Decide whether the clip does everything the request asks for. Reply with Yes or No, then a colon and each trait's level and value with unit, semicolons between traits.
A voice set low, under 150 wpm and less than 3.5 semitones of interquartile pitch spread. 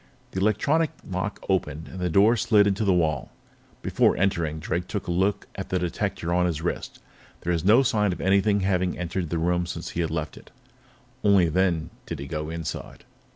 No: very low, 90 Hz; average, 200 wpm; average, 3.0 semitones